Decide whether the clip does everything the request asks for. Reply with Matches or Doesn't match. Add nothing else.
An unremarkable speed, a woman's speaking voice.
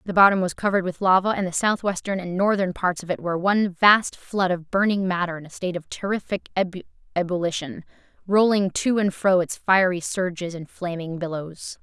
Matches